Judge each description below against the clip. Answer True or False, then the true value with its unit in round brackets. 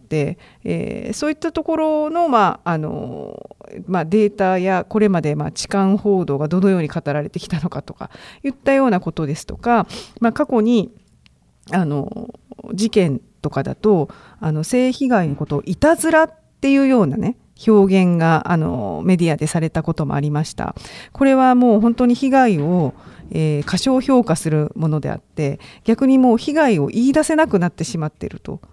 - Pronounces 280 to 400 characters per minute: True (340 characters per minute)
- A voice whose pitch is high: True (200 Hz)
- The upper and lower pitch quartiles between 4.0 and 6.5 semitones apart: False (7.6 semitones)